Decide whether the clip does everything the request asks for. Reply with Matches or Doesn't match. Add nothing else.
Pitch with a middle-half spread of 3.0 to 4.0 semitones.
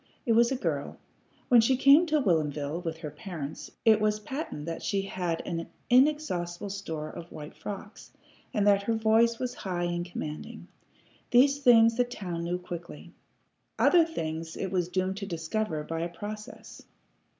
Doesn't match